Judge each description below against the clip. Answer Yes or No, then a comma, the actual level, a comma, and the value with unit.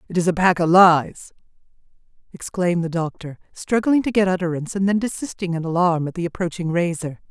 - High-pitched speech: No, medium, 175 Hz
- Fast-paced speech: No, average, 180 wpm